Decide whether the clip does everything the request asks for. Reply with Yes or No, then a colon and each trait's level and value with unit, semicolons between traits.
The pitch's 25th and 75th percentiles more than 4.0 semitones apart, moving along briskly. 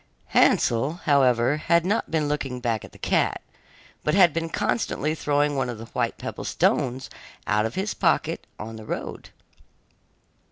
No: average, 5.1 semitones; average, 160 wpm